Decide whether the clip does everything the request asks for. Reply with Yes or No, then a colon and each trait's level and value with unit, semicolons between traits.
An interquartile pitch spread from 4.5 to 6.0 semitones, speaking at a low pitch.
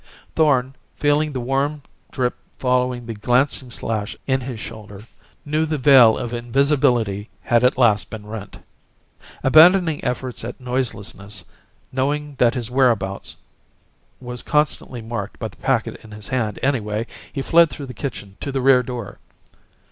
No: average, 3.5 semitones; low, 125 Hz